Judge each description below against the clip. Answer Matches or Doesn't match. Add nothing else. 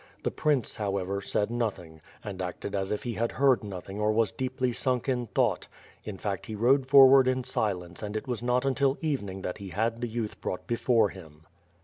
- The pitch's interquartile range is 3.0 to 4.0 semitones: Doesn't match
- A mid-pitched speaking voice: Doesn't match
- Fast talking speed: Matches